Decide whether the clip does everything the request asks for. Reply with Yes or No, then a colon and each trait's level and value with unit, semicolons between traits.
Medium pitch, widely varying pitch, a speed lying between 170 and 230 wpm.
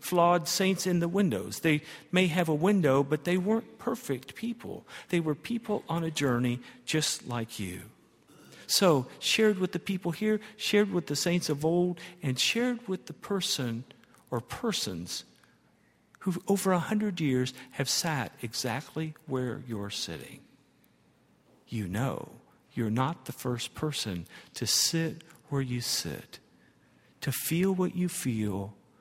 No: medium, 160 Hz; wide, 6.3 semitones; average, 145 wpm